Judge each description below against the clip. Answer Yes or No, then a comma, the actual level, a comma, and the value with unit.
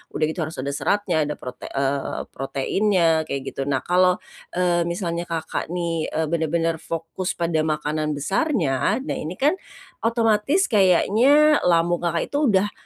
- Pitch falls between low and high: Yes, medium, 170 Hz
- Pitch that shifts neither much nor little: Yes, average, 4.1 semitones